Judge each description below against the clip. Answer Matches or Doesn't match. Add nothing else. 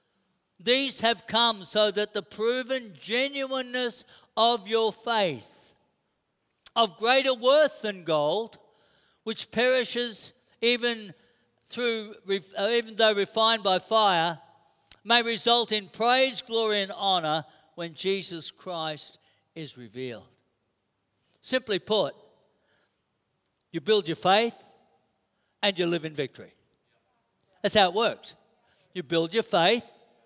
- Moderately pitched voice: Doesn't match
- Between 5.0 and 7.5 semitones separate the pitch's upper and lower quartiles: Matches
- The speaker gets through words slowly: Matches